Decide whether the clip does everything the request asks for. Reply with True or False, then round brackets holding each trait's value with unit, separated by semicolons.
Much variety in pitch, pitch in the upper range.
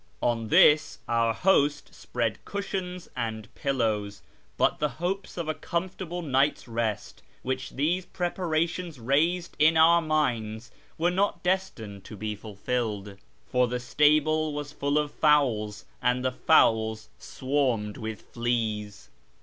False (6.3 semitones; 135 Hz)